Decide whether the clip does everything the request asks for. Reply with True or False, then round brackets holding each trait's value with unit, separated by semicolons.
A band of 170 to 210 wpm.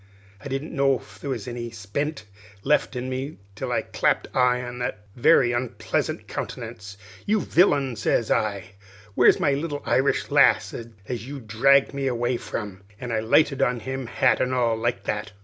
True (175 wpm)